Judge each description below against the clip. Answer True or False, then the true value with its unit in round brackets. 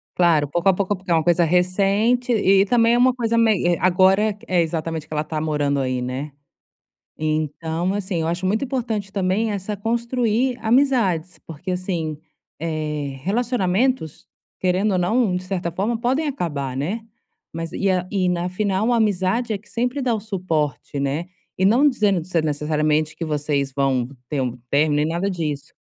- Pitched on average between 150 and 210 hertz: True (185 Hz)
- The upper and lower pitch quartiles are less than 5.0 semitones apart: False (5.6 semitones)